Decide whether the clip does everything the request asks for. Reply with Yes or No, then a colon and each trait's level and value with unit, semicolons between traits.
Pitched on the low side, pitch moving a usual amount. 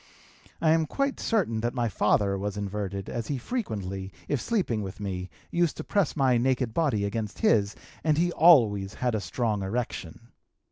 No: low, 115 Hz; wide, 6.7 semitones